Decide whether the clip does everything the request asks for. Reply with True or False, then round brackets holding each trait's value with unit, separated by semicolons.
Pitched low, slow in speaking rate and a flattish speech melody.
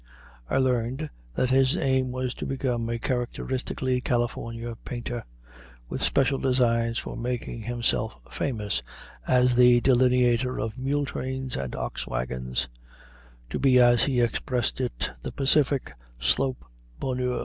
True (125 Hz; 130 wpm; 1.9 semitones)